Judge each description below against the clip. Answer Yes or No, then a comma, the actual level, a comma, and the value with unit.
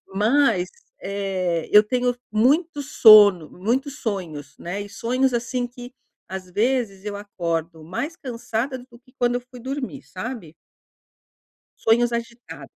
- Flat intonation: No, average, 4.6 semitones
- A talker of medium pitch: No, high, 230 Hz